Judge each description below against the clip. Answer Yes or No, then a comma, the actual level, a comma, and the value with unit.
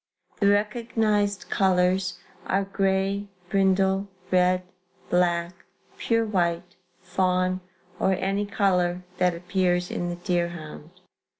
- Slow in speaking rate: Yes, slow, 100 wpm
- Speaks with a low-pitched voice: No, medium, 185 Hz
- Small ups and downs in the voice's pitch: Yes, narrow, 1.9 semitones